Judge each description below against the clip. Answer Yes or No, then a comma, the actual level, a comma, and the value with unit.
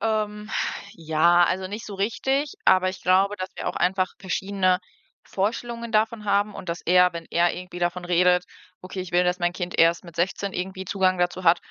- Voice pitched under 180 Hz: No, medium, 185 Hz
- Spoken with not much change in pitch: Yes, narrow, 2.3 semitones